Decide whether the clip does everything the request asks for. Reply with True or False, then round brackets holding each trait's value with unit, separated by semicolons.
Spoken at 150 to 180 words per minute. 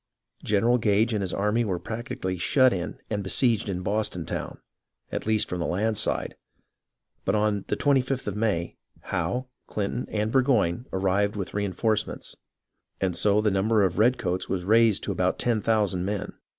True (175 wpm)